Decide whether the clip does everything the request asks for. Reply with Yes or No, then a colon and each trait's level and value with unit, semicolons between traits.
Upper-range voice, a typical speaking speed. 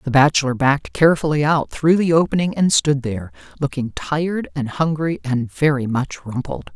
No: medium, 140 Hz; average, 170 wpm